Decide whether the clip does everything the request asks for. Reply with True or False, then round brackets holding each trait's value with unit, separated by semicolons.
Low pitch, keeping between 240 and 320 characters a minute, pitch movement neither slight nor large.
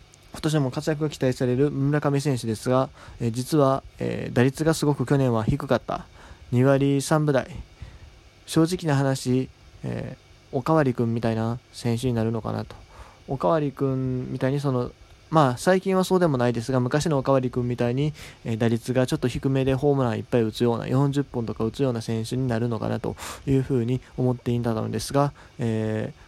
False (130 Hz; 370 characters per minute; 3.5 semitones)